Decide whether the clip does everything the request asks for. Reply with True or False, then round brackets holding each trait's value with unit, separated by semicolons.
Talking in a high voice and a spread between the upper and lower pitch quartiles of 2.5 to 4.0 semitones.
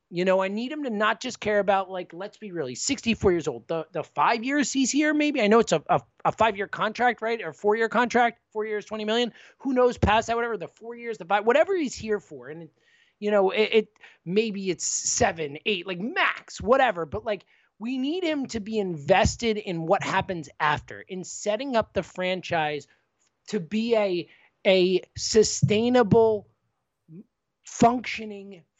True (210 Hz; 3.7 semitones)